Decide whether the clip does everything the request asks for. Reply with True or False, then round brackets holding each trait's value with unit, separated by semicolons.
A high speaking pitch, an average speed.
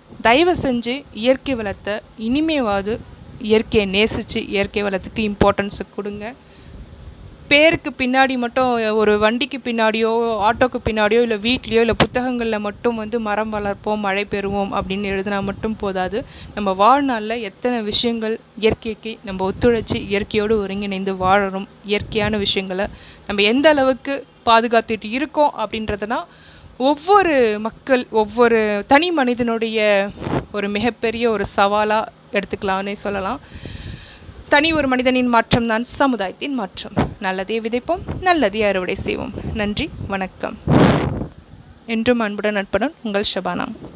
True (220 Hz; 110 wpm)